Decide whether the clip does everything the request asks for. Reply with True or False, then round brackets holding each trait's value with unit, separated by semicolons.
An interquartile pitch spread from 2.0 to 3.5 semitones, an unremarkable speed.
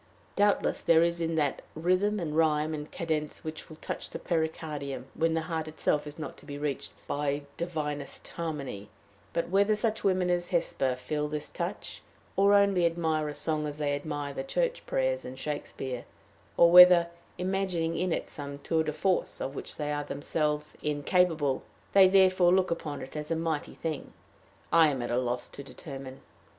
True (3.1 semitones; 180 wpm)